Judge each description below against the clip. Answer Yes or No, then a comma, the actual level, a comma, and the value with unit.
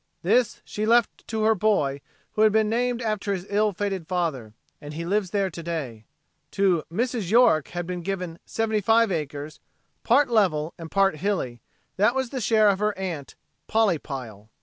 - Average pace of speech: Yes, average, 180 wpm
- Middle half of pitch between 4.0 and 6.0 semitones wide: Yes, average, 5.1 semitones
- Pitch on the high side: Yes, high, 195 Hz